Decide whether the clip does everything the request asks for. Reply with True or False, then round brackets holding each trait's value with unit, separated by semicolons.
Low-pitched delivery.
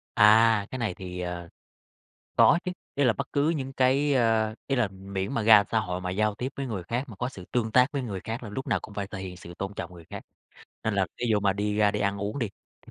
True (105 Hz)